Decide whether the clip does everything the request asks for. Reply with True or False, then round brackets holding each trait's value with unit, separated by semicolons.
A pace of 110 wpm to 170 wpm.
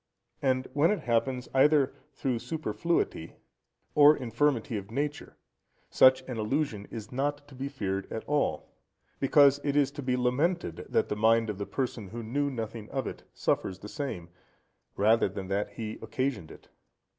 True (165 wpm)